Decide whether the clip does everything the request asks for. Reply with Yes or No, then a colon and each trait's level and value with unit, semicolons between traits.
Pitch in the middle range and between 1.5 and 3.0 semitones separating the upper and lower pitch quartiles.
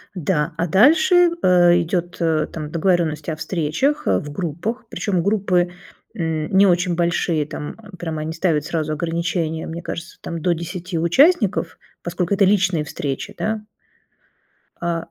Yes: medium, 170 Hz; average, 2.7 semitones